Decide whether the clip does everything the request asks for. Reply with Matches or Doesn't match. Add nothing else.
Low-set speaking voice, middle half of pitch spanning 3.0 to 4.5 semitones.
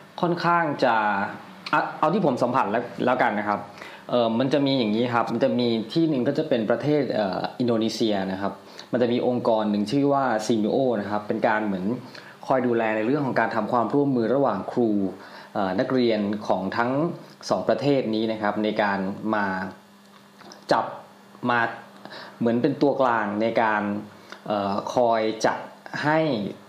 Matches